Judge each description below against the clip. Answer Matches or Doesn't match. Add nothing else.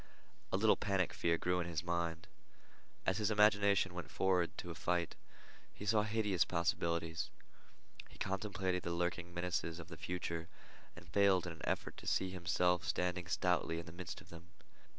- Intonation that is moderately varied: Doesn't match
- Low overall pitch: Matches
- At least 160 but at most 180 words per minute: Matches